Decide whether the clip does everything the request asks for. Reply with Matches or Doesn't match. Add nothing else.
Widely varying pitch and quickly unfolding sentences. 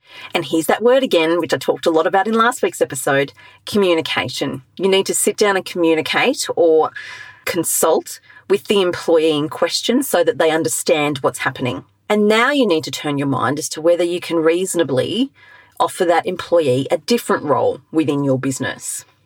Doesn't match